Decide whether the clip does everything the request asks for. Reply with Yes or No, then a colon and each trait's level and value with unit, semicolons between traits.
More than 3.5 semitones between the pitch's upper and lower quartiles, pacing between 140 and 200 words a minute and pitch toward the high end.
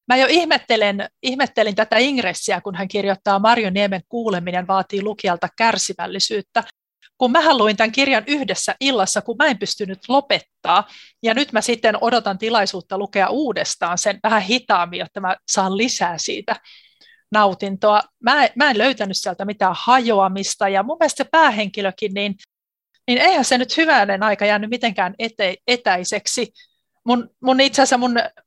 Yes: average, 4.2 semitones; average, 150 wpm; high, 215 Hz